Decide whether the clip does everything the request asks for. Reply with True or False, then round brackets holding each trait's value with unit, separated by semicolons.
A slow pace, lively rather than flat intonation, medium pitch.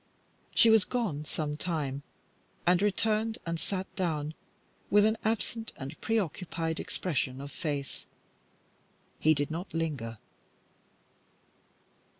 True (115 wpm; 5.8 semitones; 165 Hz)